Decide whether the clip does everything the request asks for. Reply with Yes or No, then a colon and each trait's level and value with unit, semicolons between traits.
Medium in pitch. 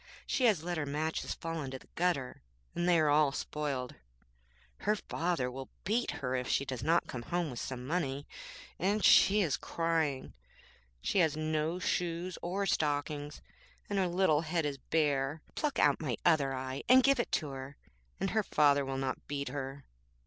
Yes: medium, 155 Hz